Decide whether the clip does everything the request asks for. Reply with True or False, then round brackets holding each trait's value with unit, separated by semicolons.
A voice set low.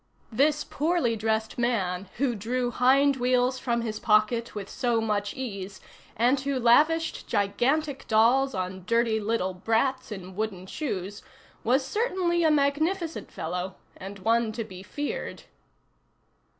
False (235 Hz)